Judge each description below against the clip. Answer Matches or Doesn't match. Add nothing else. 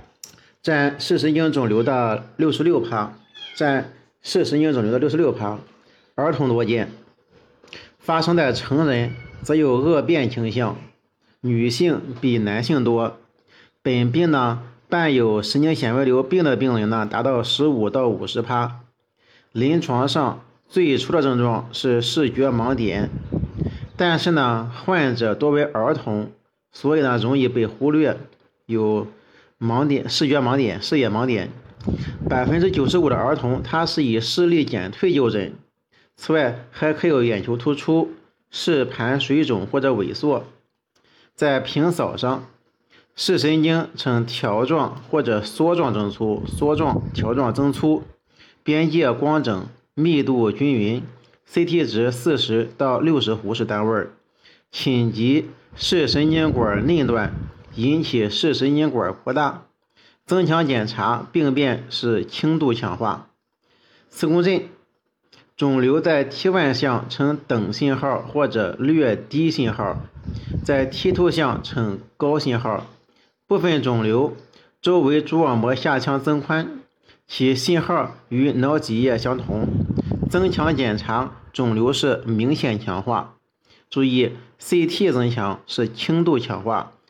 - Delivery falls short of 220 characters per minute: Matches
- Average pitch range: Matches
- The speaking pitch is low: Matches